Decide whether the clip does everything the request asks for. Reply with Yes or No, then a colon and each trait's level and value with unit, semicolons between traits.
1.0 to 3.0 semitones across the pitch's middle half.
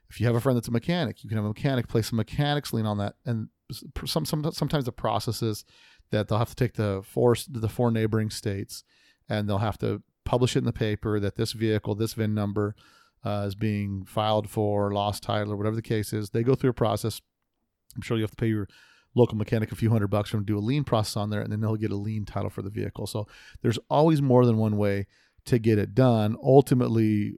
Yes: narrow, 2.5 semitones